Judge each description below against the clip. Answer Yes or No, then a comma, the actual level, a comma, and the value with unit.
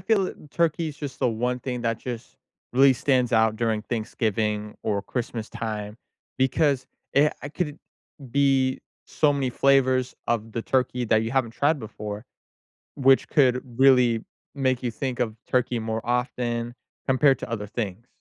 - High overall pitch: No, low, 125 Hz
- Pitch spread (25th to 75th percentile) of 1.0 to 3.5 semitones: Yes, average, 3.1 semitones